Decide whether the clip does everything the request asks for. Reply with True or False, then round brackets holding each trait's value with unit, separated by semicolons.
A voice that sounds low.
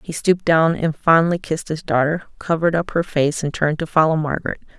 False (160 Hz)